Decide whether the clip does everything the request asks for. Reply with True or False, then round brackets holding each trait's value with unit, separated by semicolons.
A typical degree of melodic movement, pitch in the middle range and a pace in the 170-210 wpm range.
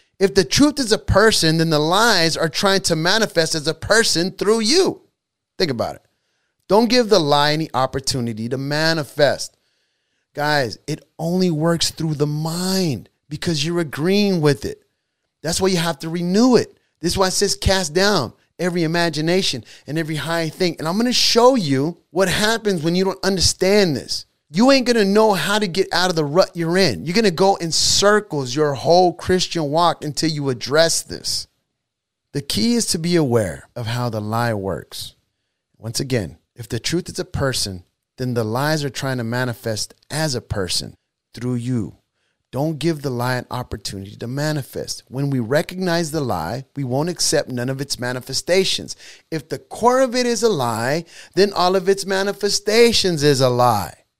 False (6.5 semitones; 160 Hz; 185 wpm)